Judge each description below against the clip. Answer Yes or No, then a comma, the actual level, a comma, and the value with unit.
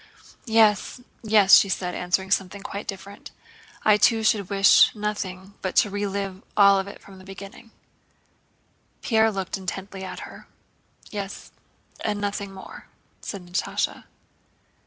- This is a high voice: Yes, high, 200 Hz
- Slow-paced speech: Yes, slow, 130 wpm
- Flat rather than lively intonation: Yes, narrow, 1.5 semitones